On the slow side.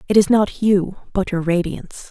No: average, 200 wpm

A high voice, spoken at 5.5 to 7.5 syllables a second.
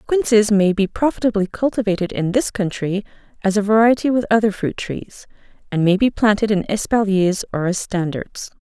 No: high, 205 Hz; 5.2 syllables/s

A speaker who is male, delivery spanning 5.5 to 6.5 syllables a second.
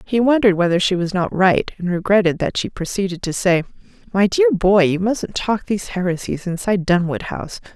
No: female; 5.6 syllables/s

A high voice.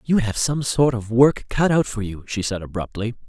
No: low, 120 Hz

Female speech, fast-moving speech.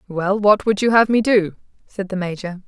Yes: female; fast, 225 wpm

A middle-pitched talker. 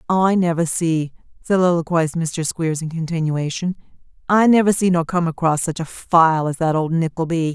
Yes: medium, 165 Hz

